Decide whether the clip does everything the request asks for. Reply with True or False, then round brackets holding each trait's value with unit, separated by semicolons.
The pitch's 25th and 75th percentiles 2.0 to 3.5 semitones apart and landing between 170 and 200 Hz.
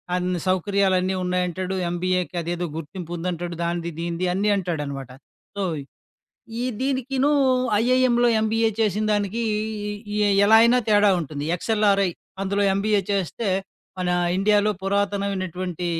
True (3.0 semitones; 190 Hz)